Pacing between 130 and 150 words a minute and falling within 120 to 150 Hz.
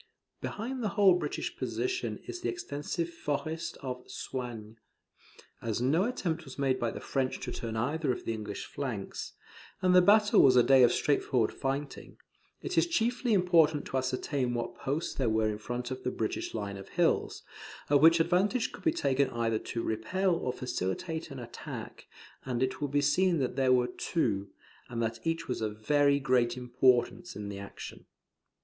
No: average, 180 wpm; low, 135 Hz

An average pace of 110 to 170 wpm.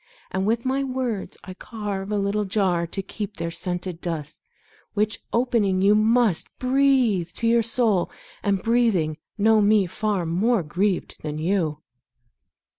Yes: average, 145 wpm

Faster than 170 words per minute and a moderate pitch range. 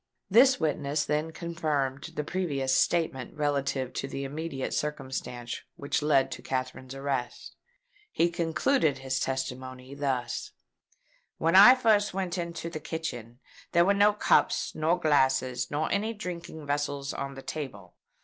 No: average, 140 wpm; average, 4.2 semitones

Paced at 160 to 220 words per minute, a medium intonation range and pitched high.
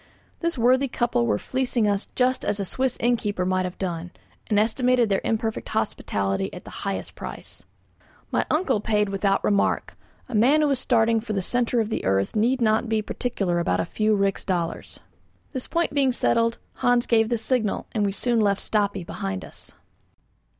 Yes: average, 185 wpm; average, 3.9 semitones; high, 220 Hz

